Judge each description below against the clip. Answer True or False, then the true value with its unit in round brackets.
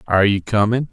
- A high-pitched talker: False (110 Hz)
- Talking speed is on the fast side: False (195 wpm)